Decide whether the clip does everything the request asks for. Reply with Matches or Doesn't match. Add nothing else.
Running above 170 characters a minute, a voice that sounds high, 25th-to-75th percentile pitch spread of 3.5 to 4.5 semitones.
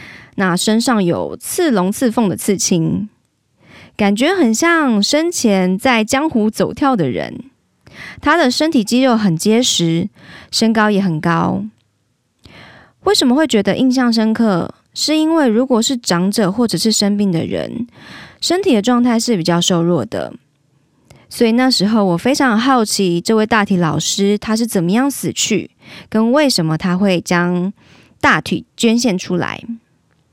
Doesn't match